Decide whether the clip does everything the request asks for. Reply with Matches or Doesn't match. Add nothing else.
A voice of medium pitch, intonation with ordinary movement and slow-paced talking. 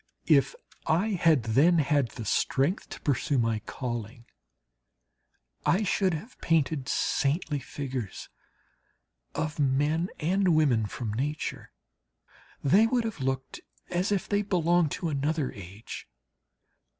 Matches